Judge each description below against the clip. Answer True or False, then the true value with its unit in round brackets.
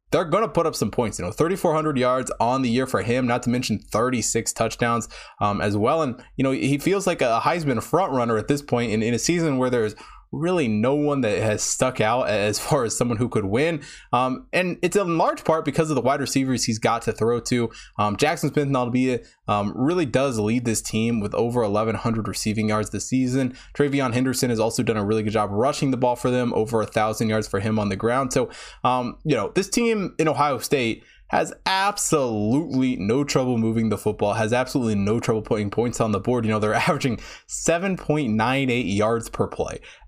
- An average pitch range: True (4.5 semitones)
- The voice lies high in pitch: False (125 Hz)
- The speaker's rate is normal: False (225 wpm)